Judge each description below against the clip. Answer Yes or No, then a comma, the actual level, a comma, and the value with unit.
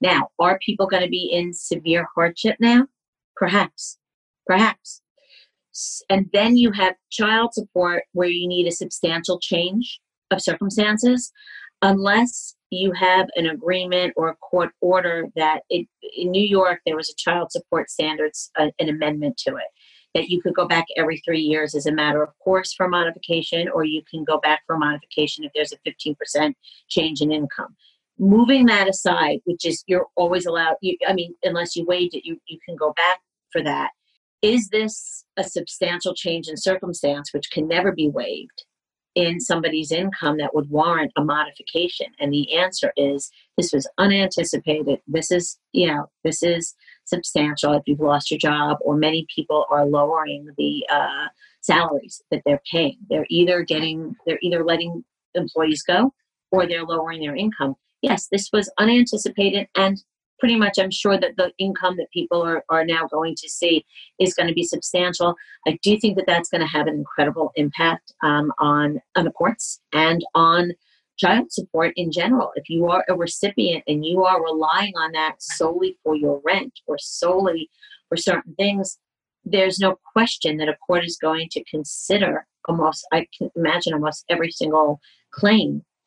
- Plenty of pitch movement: No, average, 3.4 semitones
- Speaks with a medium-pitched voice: Yes, medium, 175 Hz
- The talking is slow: No, average, 175 wpm